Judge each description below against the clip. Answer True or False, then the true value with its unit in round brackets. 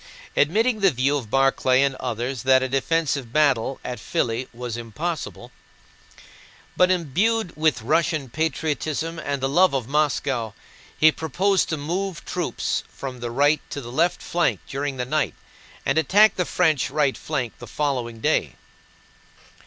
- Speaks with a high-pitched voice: False (145 Hz)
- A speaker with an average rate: True (150 wpm)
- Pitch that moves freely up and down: False (4.2 semitones)